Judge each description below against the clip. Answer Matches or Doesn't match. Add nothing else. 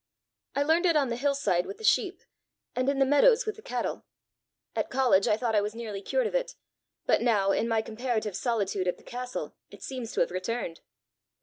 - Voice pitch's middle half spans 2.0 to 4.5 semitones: Doesn't match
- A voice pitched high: Matches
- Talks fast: Matches